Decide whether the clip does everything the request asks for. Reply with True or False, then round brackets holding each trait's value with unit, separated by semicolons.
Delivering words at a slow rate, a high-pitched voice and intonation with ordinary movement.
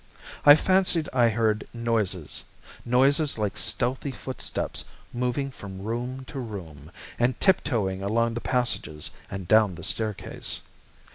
False (125 wpm; 115 Hz; 4.5 semitones)